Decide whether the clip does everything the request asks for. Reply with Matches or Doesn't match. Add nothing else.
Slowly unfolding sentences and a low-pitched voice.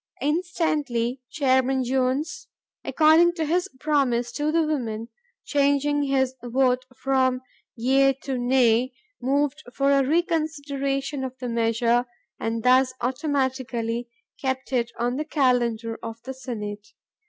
Doesn't match